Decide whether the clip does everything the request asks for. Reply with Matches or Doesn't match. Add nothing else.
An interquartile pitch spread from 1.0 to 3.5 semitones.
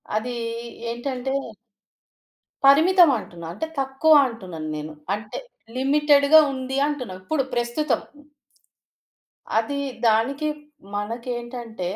Doesn't match